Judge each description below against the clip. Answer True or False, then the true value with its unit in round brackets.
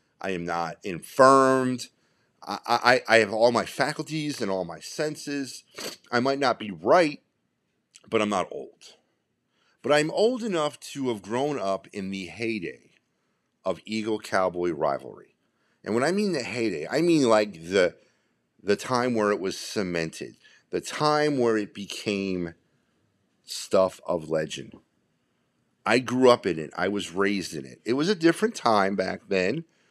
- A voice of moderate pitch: False (115 Hz)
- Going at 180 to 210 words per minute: False (160 wpm)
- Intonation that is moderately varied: False (6.1 semitones)